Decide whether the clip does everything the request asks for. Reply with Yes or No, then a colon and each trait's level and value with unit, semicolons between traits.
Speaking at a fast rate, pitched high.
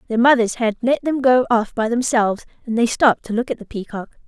Yes: fast, 240 wpm; high, 235 Hz